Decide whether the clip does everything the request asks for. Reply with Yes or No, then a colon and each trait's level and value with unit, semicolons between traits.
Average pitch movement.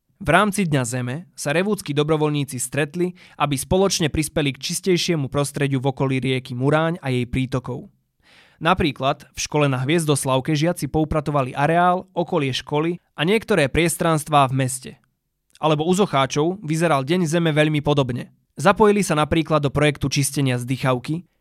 Yes: average, 3.8 semitones